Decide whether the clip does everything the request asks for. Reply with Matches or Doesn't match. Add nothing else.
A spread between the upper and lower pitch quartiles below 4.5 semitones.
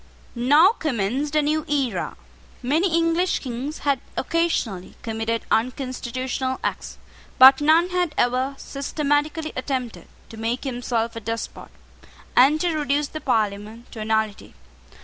Doesn't match